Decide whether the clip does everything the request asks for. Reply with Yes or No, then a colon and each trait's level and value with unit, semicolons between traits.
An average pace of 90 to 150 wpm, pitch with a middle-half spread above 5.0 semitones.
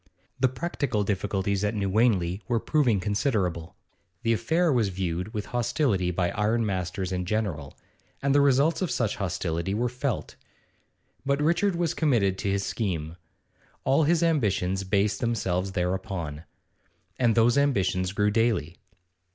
Yes: average, 140 wpm; wide, 5.4 semitones